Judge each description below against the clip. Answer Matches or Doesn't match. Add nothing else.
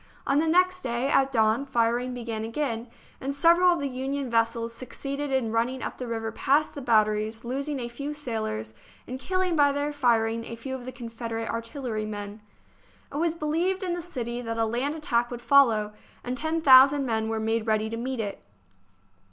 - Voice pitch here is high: Matches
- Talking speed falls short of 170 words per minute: Doesn't match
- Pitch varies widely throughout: Doesn't match